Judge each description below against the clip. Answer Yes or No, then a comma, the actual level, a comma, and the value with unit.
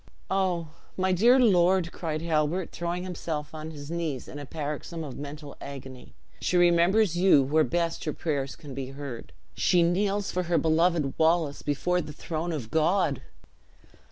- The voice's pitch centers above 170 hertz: No, medium, 165 Hz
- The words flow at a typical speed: Yes, average, 160 wpm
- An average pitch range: Yes, average, 3.3 semitones